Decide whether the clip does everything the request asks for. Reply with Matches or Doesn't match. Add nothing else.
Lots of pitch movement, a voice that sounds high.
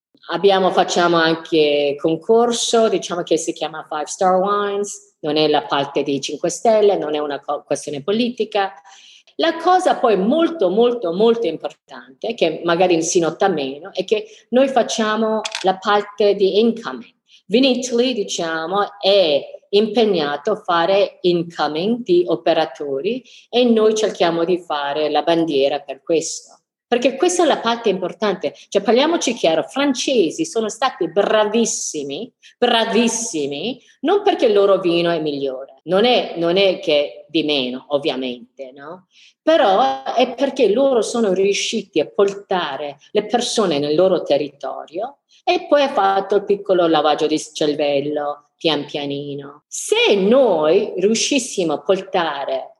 Matches